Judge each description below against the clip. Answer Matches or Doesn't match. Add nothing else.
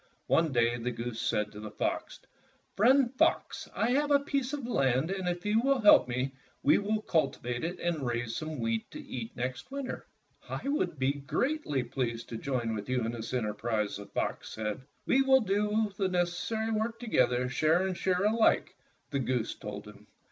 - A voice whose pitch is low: Doesn't match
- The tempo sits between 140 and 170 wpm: Doesn't match